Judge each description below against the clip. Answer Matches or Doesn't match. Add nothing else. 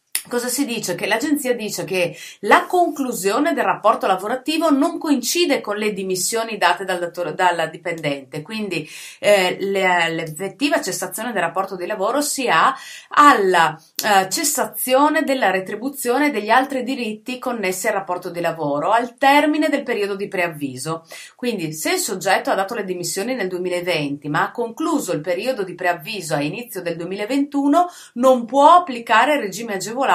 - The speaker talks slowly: Doesn't match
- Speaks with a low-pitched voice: Doesn't match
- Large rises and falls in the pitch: Matches